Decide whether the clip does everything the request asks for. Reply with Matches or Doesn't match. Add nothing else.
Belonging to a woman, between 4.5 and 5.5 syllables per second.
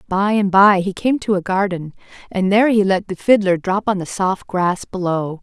Matches